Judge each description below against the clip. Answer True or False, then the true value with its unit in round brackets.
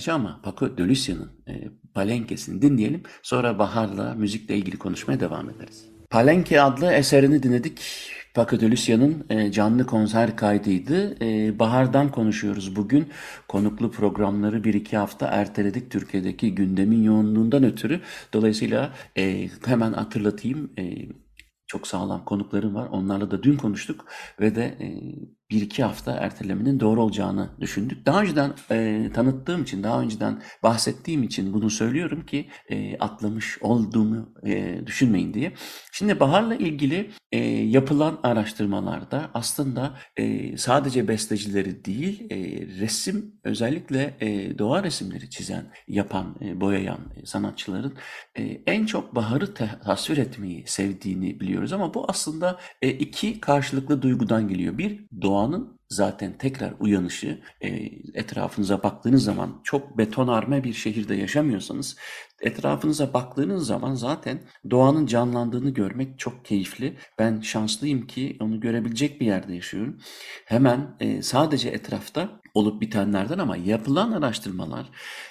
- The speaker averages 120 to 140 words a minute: True (125 wpm)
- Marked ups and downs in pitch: False (5.0 semitones)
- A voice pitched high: False (110 Hz)